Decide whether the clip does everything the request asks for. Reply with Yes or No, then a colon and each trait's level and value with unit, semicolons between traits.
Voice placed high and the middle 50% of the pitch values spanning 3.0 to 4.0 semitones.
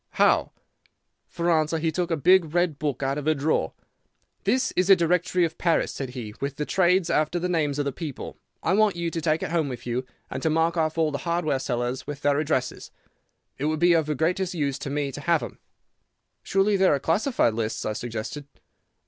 No: medium, 155 Hz; average, 3.6 semitones